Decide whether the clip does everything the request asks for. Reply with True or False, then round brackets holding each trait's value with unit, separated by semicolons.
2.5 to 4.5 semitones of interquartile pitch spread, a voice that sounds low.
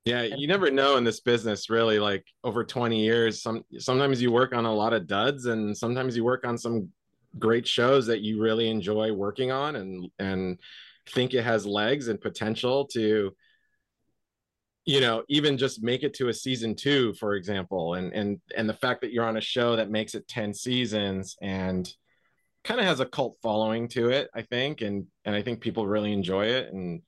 True (2.9 semitones; 115 Hz)